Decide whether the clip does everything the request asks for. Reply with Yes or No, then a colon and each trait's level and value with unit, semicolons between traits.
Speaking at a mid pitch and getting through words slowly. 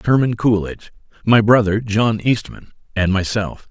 No: low, 110 Hz; slow, 130 wpm